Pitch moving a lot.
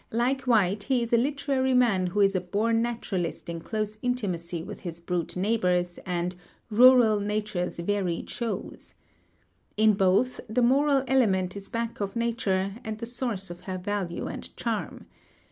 No: average, 4.4 semitones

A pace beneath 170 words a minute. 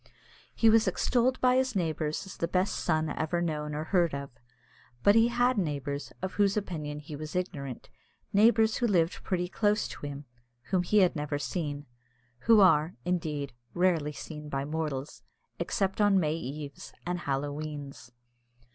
Yes: average, 160 wpm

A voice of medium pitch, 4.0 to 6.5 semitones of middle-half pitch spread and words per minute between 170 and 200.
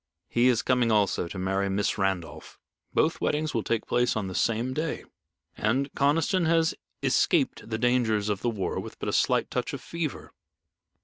No: low, 115 Hz; average, 5.1 semitones; average, 175 wpm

